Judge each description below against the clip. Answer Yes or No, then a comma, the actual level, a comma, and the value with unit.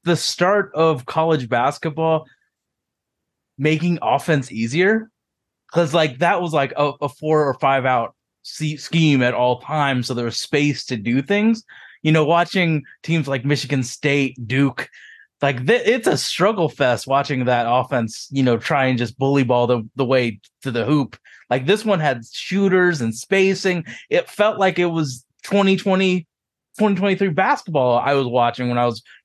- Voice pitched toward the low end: No, medium, 150 Hz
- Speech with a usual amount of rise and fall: No, wide, 5.7 semitones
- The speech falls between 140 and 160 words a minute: No, average, 170 wpm